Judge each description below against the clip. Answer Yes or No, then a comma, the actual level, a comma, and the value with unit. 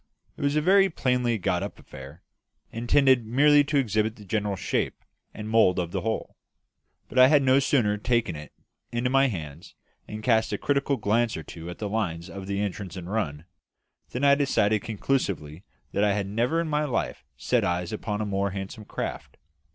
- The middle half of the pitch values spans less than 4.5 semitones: No, average, 4.9 semitones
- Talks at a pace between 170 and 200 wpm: Yes, average, 190 wpm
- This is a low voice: Yes, low, 110 Hz